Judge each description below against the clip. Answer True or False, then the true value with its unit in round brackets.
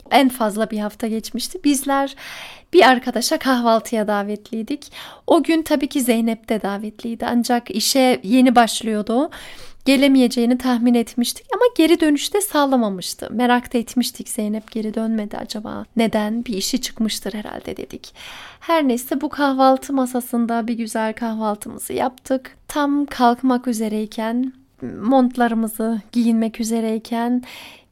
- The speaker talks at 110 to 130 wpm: True (120 wpm)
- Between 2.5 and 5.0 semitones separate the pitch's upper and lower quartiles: True (2.9 semitones)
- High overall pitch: True (240 Hz)